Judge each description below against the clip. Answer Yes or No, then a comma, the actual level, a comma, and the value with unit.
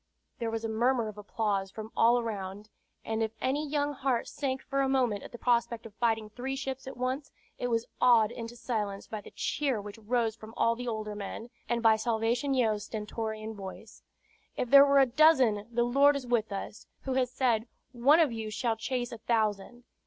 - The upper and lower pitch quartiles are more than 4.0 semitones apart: No, average, 2.9 semitones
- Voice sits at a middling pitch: No, high, 235 Hz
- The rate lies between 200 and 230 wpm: Yes, fast, 205 wpm